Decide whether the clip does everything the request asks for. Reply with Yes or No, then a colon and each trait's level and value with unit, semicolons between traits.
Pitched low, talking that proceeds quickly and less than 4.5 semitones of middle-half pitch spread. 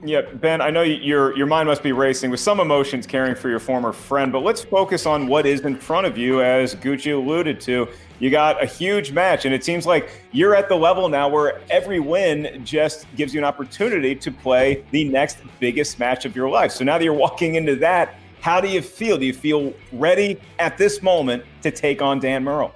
No: medium, 145 Hz; fast, 225 wpm; average, 3.5 semitones